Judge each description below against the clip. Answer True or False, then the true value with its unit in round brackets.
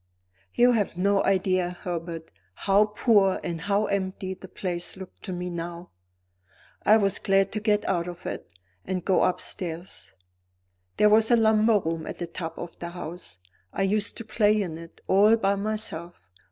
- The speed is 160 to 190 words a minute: True (170 wpm)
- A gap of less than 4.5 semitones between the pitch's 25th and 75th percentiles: True (3.2 semitones)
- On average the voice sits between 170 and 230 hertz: True (190 Hz)